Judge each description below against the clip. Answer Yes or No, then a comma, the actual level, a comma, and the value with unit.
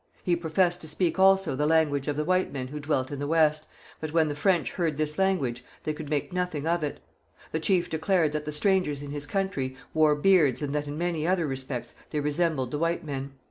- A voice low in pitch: No, medium, 155 Hz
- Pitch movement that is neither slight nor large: Yes, average, 3.1 semitones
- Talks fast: Yes, fast, 225 wpm